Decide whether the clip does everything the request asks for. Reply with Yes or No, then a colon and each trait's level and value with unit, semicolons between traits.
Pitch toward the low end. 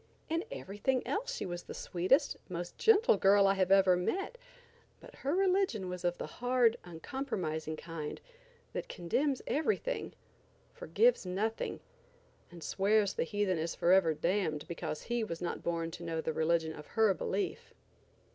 No: high, 190 Hz